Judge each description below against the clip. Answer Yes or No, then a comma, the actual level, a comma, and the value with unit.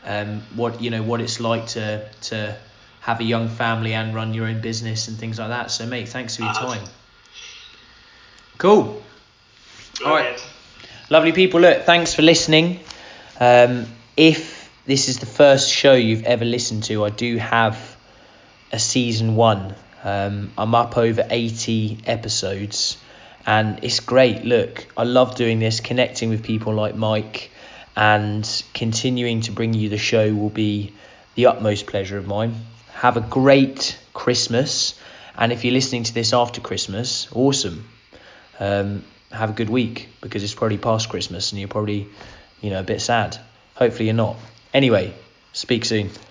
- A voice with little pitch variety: Yes, narrow, 2.3 semitones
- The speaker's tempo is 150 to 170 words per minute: Yes, average, 160 wpm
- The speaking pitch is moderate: No, low, 115 Hz